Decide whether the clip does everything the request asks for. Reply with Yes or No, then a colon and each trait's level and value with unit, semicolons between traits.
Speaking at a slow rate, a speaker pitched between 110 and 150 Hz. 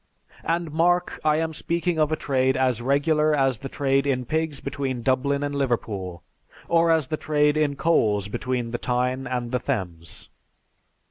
No: average, 165 wpm; medium, 140 Hz